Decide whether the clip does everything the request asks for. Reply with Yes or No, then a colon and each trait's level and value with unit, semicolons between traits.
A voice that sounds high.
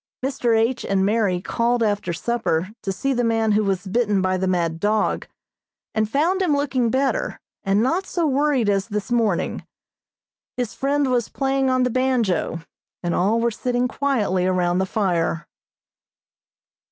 Yes: high, 225 Hz